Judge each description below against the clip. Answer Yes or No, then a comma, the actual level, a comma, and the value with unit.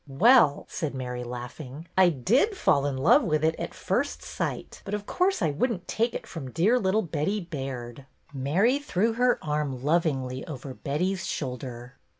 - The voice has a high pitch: No, medium, 155 Hz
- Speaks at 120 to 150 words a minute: No, average, 175 wpm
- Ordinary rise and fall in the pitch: No, wide, 7.3 semitones